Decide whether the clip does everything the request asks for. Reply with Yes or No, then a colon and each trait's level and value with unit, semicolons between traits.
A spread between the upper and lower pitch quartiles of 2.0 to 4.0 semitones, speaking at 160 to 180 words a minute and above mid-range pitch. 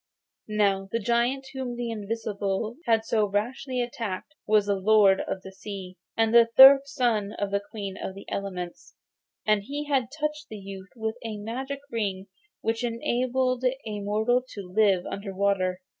Yes: average, 3.5 semitones; average, 165 wpm; high, 215 Hz